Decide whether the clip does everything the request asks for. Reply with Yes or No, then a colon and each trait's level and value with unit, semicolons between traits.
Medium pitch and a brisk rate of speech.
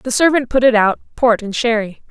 No: high, 235 Hz; fast, 230 wpm